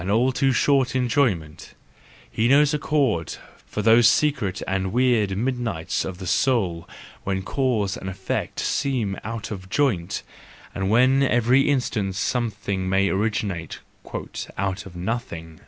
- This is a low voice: Yes, low, 110 Hz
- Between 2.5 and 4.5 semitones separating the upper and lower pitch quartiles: No, average, 5.1 semitones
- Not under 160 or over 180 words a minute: No, slow, 135 wpm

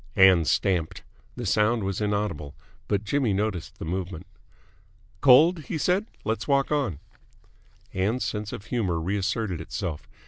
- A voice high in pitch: No, low, 105 Hz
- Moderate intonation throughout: Yes, average, 4.5 semitones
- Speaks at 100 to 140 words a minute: Yes, slow, 135 wpm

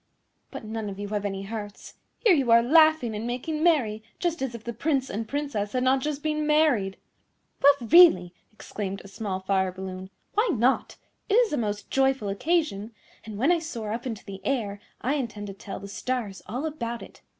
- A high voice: Yes, high, 235 Hz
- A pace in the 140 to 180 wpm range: No, average, 200 wpm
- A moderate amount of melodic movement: No, wide, 6.0 semitones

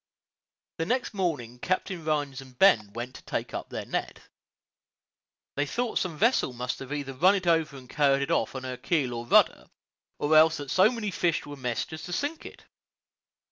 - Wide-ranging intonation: Yes, wide, 5.8 semitones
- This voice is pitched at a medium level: Yes, medium, 145 Hz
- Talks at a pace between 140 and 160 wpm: No, average, 195 wpm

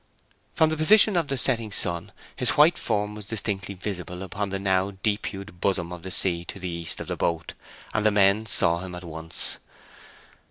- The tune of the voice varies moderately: Yes, average, 3.4 semitones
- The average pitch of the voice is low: Yes, low, 100 Hz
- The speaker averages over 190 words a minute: Yes, average, 200 wpm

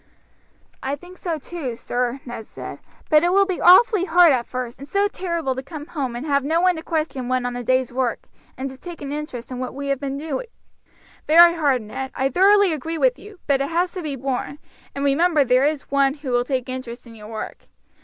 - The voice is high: Yes, very high, 280 Hz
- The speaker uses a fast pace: Yes, fast, 230 wpm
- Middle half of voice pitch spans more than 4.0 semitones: Yes, average, 4.8 semitones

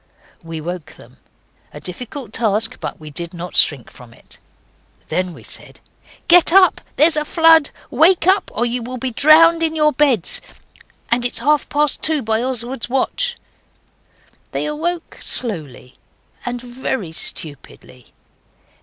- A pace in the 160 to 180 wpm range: No, average, 145 wpm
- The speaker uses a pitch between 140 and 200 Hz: No, very high, 250 Hz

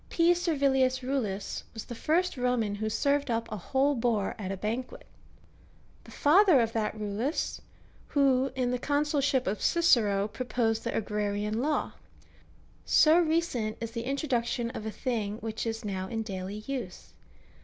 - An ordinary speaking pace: Yes, average, 155 wpm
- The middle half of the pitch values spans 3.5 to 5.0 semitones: Yes, average, 4.5 semitones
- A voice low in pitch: No, high, 240 Hz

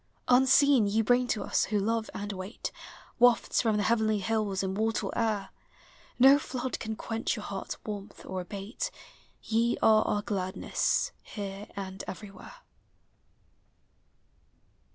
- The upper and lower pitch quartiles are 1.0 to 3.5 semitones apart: Yes, average, 2.7 semitones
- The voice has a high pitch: Yes, high, 215 Hz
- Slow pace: Yes, slow, 130 wpm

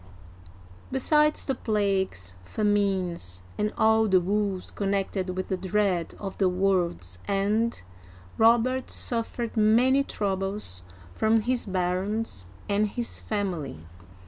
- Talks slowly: Yes, slow, 110 wpm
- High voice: Yes, high, 200 Hz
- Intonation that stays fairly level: No, average, 3.2 semitones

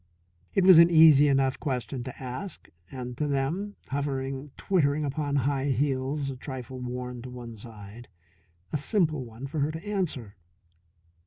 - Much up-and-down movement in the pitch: No, average, 3.1 semitones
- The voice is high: No, low, 135 Hz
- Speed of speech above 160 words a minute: No, average, 155 wpm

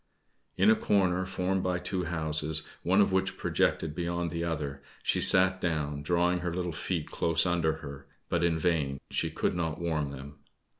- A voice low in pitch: Yes, very low, 85 Hz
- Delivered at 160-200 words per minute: Yes, average, 180 wpm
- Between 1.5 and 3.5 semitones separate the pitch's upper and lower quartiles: Yes, average, 2.7 semitones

